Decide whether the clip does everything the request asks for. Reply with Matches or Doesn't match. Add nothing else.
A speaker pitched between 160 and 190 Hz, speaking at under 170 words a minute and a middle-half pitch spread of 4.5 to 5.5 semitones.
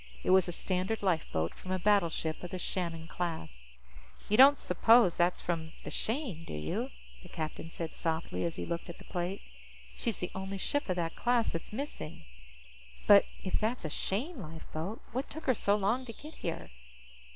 Doesn't match